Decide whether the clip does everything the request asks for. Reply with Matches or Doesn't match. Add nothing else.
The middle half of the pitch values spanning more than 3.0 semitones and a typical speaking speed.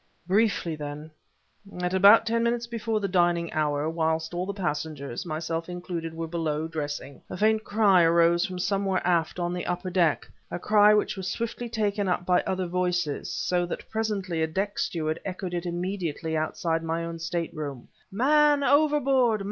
Matches